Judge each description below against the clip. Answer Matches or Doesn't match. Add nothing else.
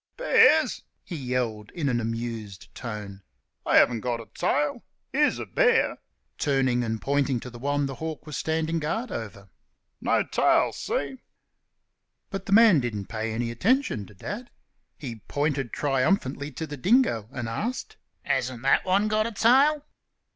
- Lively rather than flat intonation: Matches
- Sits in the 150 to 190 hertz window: Doesn't match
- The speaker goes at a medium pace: Matches